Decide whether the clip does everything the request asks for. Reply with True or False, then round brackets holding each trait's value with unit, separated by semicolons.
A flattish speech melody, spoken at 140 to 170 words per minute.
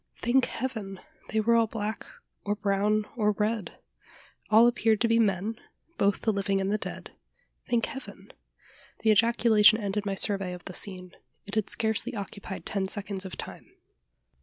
True (2.3 semitones; 160 wpm)